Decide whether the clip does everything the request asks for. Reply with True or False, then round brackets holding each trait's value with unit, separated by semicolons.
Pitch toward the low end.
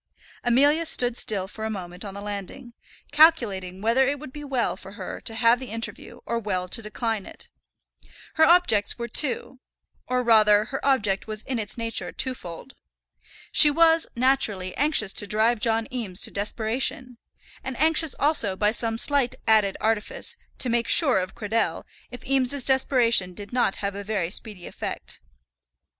False (230 Hz)